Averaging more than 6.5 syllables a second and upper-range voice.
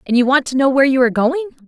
Yes: 8.5 syllables/s; very high, 265 Hz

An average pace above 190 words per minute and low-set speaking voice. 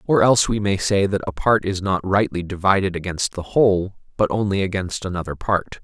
Yes: fast, 205 wpm; very low, 95 Hz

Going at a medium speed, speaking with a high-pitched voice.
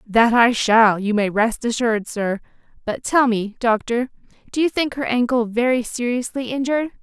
Yes: average, 170 wpm; high, 235 Hz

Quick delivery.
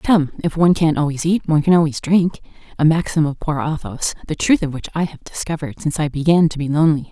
Yes: fast, 230 wpm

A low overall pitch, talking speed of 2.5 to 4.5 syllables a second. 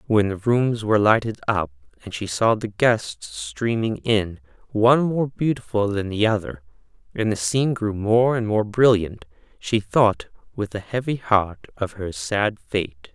Yes: low, 105 Hz; 4.2 syllables/s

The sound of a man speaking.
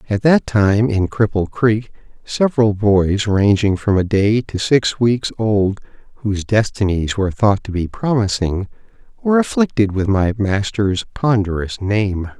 Yes: male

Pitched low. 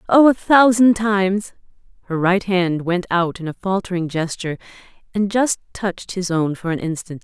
No: high, 190 Hz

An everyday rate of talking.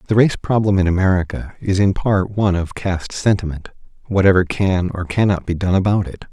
Yes: average, 190 wpm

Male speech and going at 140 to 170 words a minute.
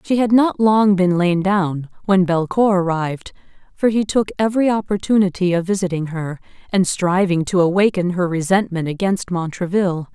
No: female; average, 155 wpm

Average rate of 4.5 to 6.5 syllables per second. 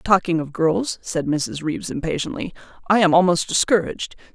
Yes: 5.3 syllables/s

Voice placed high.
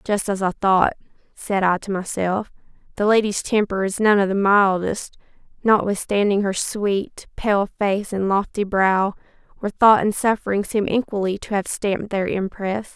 Yes: high, 200 Hz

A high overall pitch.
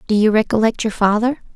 Yes: high, 220 Hz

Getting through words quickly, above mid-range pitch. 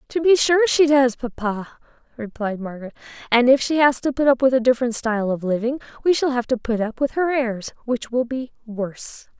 Yes: fast, 215 wpm; very high, 250 Hz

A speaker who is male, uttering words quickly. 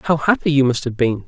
Yes: male; fast, 285 wpm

